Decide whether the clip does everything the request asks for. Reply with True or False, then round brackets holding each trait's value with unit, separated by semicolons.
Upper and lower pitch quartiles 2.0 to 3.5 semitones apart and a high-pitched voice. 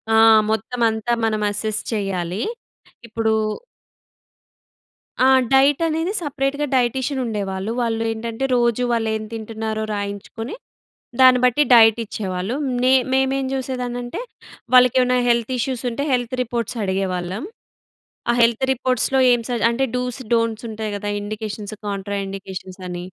True (3.2 semitones; 230 Hz)